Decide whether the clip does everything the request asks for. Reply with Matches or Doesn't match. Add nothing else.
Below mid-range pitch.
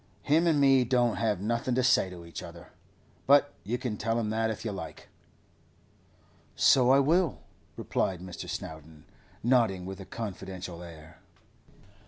Matches